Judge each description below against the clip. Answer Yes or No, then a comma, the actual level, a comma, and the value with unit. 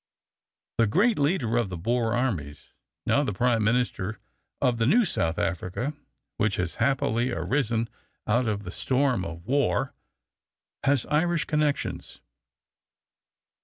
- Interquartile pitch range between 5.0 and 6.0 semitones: Yes, wide, 5.4 semitones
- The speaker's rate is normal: No, slow, 130 wpm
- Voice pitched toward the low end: Yes, low, 120 Hz